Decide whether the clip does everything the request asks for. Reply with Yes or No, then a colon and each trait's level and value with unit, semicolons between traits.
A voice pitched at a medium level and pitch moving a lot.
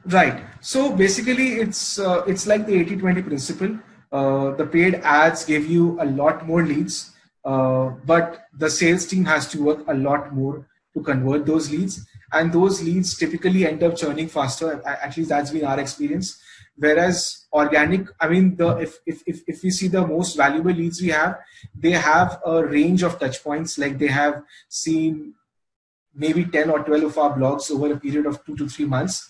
No: medium, 160 Hz; average, 3.2 semitones